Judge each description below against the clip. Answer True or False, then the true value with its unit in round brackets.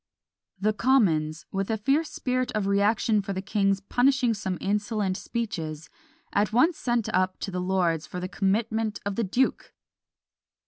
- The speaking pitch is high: True (205 Hz)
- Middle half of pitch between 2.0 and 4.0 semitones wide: True (3.4 semitones)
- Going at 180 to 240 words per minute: False (155 wpm)